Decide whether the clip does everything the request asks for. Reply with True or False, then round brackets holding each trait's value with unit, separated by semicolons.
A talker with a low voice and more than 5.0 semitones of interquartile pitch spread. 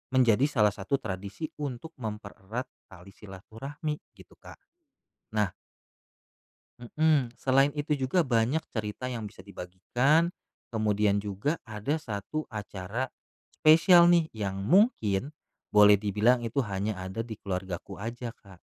True (110 Hz; 5.5 semitones)